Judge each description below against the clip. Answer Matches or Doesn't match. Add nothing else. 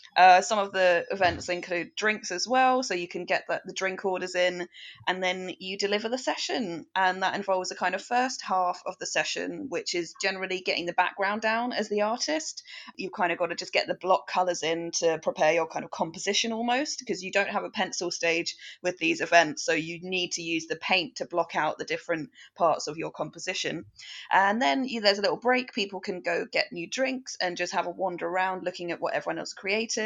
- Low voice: Doesn't match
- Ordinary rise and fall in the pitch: Matches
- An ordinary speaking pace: Doesn't match